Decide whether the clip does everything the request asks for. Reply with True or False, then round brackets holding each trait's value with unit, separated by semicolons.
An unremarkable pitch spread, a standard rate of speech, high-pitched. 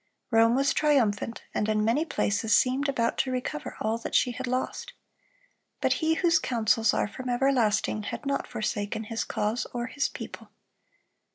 True (3.6 semitones; 165 wpm; 240 Hz)